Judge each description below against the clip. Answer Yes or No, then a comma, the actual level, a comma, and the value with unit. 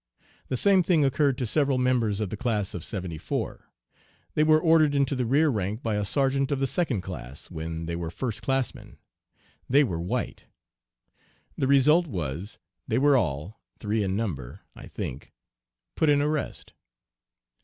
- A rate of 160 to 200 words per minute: Yes, average, 165 wpm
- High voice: No, low, 125 Hz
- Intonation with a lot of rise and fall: Yes, wide, 7.2 semitones